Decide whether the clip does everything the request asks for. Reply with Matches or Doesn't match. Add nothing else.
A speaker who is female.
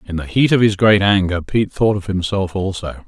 Doesn't match